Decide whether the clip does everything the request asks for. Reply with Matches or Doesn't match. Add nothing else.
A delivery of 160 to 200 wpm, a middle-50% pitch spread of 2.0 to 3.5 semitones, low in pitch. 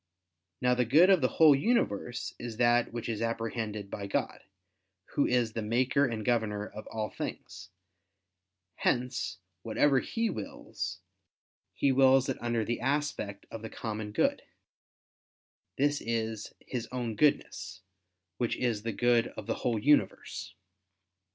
Doesn't match